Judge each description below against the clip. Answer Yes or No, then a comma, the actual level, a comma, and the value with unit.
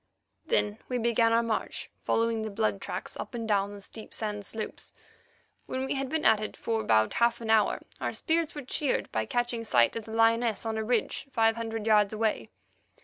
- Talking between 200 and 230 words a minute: Yes, fast, 205 wpm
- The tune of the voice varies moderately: No, narrow, 1.9 semitones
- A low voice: No, high, 225 Hz